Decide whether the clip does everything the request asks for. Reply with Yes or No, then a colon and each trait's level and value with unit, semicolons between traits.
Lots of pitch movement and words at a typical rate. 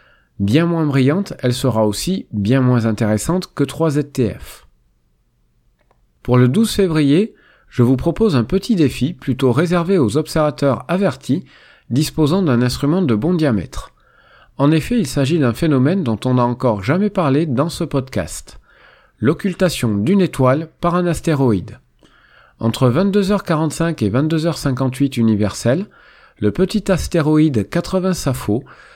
No: wide, 5.8 semitones; slow, 130 wpm